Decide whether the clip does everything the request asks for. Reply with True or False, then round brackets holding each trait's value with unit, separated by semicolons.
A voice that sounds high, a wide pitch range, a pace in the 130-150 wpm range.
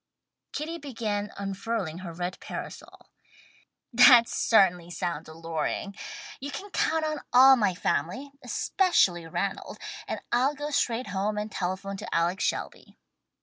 True (205 Hz; 6.8 semitones; 135 wpm)